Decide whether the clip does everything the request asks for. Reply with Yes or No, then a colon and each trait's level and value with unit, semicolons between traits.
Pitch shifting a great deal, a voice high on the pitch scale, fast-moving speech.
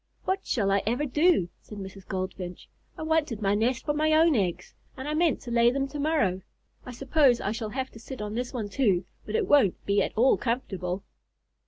Yes: wide, 6.4 semitones; high, 240 Hz; fast, 215 wpm